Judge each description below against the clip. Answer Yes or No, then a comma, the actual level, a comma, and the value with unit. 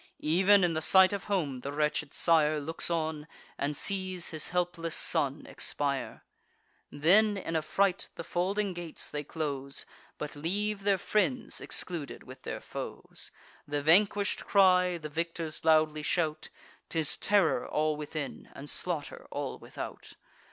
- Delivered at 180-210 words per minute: No, average, 145 wpm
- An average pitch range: Yes, average, 3.8 semitones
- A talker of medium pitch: Yes, medium, 165 Hz